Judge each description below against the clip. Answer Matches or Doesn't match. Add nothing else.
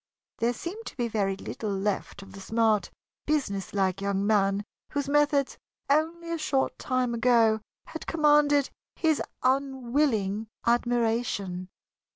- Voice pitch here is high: Matches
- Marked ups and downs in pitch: Matches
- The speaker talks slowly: Matches